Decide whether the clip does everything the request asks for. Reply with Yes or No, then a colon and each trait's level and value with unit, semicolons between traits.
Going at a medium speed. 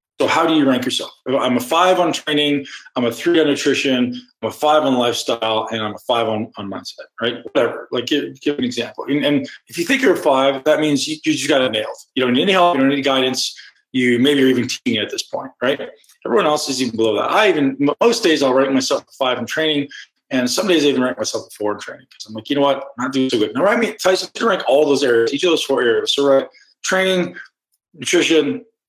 No: fast, 265 wpm